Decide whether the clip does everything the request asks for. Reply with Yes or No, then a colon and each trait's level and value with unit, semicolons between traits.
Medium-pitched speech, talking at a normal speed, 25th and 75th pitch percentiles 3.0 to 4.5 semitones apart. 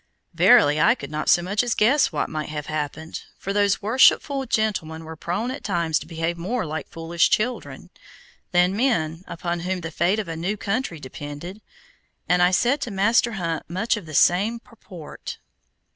No: medium, 180 Hz; average, 180 wpm; average, 5.0 semitones